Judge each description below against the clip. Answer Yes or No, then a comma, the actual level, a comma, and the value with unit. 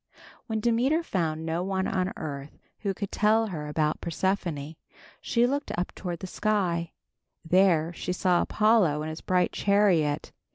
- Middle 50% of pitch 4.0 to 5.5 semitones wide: Yes, average, 4.4 semitones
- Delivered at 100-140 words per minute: No, average, 155 wpm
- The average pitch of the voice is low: No, medium, 180 Hz